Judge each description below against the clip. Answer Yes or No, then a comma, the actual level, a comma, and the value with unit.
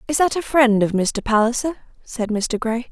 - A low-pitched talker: No, high, 240 Hz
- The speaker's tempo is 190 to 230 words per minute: Yes, fast, 205 wpm